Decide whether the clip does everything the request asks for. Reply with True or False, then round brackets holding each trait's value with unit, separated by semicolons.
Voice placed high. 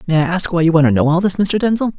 False (175 Hz)